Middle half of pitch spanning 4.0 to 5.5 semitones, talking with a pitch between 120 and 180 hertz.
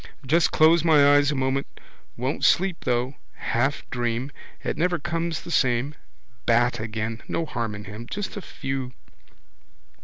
Yes: average, 5.1 semitones; low, 135 Hz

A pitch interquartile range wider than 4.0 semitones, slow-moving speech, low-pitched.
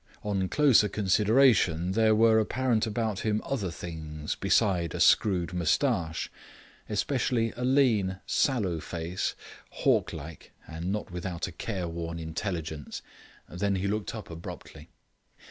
Yes: average, 4.6 semitones; slow, 125 wpm; very low, 95 Hz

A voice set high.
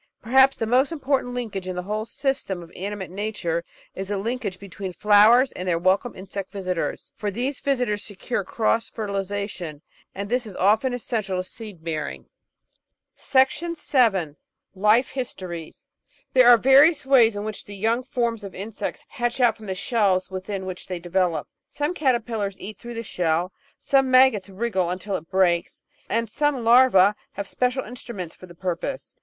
Yes: high, 210 Hz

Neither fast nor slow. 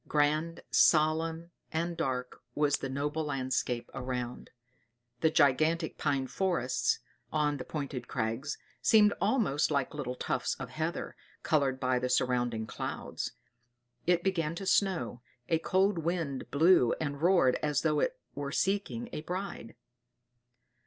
No: slow, 130 wpm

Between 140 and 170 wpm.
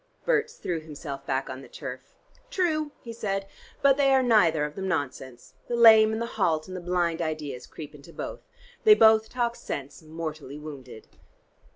No: average, 180 wpm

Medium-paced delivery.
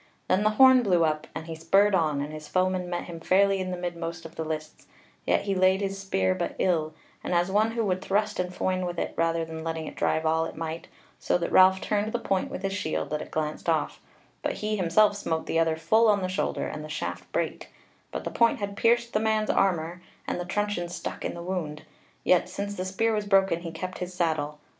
No: fast, 235 wpm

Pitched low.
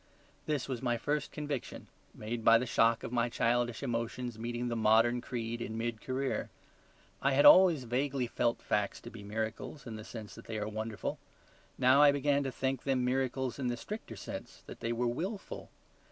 Yes: low, 120 Hz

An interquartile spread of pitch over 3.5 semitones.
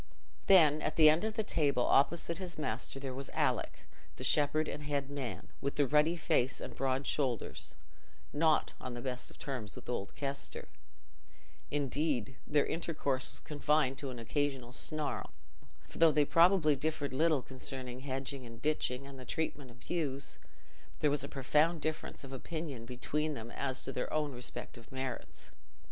No: average, 2.9 semitones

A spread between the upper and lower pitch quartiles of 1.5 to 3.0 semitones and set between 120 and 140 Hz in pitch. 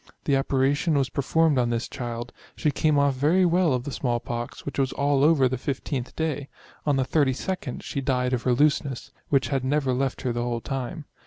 Yes: narrow, 2.5 semitones; low, 135 Hz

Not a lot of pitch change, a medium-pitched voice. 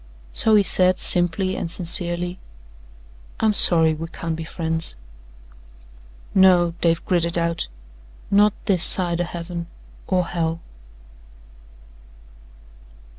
Yes: narrow, 1.8 semitones; medium, 175 Hz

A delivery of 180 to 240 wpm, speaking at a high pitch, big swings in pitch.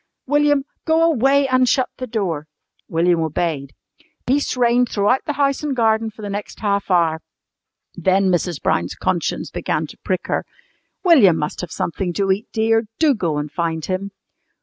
No: average, 170 wpm; high, 205 Hz; wide, 6.8 semitones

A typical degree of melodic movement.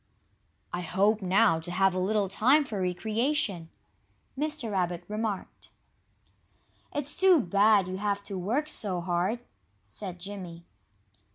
Yes: average, 3.6 semitones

